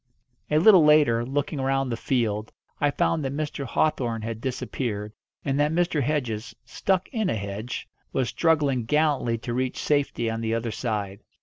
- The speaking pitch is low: Yes, low, 130 Hz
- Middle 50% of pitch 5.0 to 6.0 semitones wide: No, average, 4.5 semitones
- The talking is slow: No, average, 170 wpm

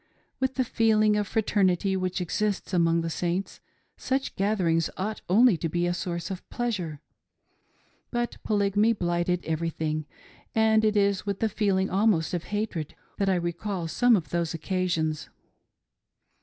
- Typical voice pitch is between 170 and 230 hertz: Yes, high, 190 Hz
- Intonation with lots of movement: No, average, 3.8 semitones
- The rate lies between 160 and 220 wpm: No, average, 145 wpm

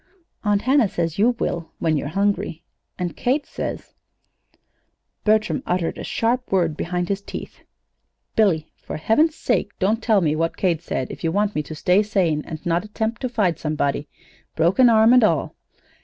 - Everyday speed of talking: Yes, average, 175 wpm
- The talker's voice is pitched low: No, high, 190 Hz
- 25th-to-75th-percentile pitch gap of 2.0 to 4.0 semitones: No, average, 5.0 semitones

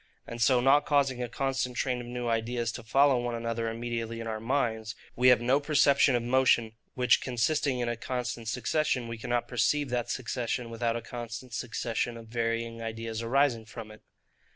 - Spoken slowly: No, average, 185 wpm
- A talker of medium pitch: No, low, 120 Hz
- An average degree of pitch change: No, narrow, 1.7 semitones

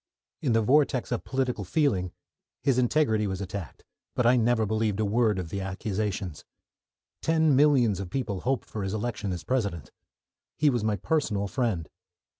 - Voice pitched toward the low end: Yes, low, 110 Hz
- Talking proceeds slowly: No, average, 165 wpm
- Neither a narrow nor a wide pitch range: Yes, average, 4.5 semitones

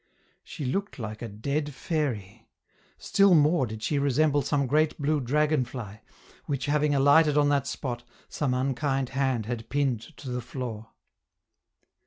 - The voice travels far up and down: No, average, 3.4 semitones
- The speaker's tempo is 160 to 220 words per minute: No, average, 150 wpm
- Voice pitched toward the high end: No, medium, 140 Hz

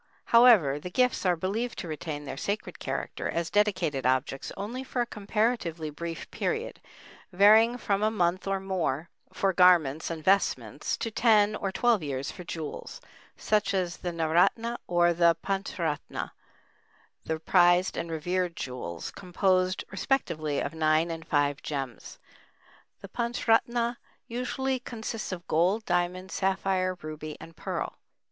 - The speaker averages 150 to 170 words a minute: No, average, 140 wpm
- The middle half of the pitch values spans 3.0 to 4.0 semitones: No, average, 4.7 semitones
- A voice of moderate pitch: Yes, medium, 180 Hz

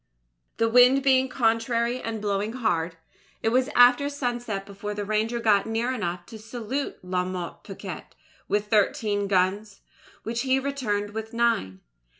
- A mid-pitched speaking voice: No, high, 225 Hz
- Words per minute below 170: Yes, average, 150 wpm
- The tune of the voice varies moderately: Yes, average, 3.3 semitones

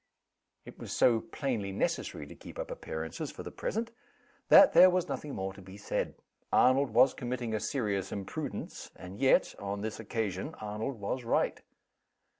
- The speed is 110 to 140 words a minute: No, average, 165 wpm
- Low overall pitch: Yes, low, 110 Hz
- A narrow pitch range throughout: No, average, 4.9 semitones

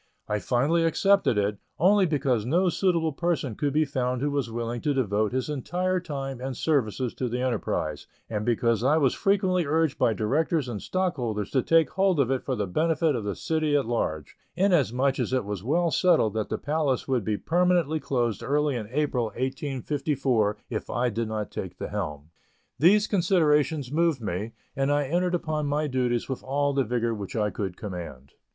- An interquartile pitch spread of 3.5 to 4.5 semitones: No, wide, 5.4 semitones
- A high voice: No, low, 135 Hz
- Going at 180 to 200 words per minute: Yes, average, 190 wpm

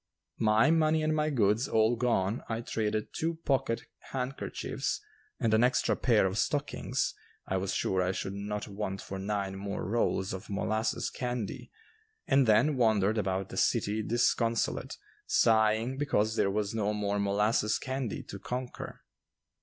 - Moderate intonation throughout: Yes, average, 3.5 semitones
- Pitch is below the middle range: Yes, low, 110 Hz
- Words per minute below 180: Yes, average, 150 wpm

